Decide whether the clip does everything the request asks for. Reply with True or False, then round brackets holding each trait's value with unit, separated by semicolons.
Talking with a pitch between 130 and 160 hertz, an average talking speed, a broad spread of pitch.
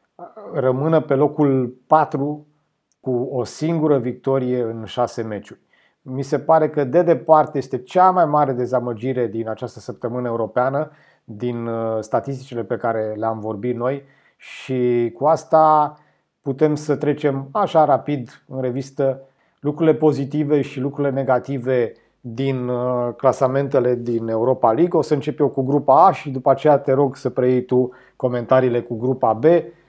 False (135 Hz; 145 wpm; 3.2 semitones)